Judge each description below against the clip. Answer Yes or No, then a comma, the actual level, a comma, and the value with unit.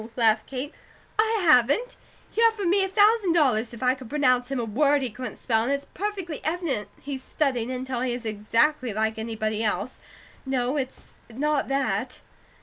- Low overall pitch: No, very high, 260 Hz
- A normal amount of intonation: Yes, average, 4.8 semitones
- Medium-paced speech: Yes, average, 175 wpm